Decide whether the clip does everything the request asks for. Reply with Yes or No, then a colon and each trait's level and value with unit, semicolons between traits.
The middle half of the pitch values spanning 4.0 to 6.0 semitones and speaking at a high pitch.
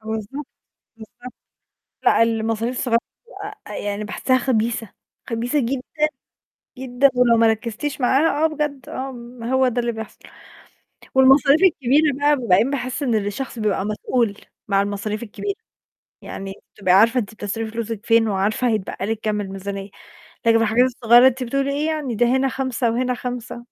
No: average, 3.2 semitones; high, 235 Hz